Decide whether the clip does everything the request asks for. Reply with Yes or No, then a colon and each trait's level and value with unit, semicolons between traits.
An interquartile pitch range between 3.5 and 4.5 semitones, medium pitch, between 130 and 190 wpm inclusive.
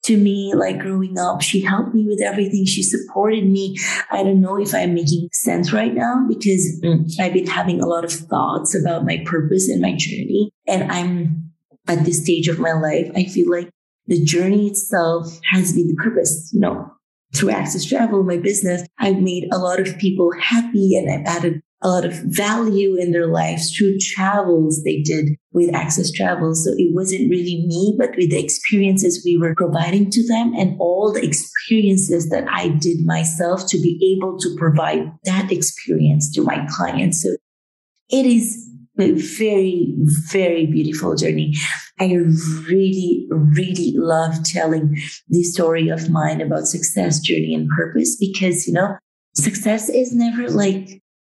No: average, 3.0 semitones; medium, 180 Hz; average, 170 wpm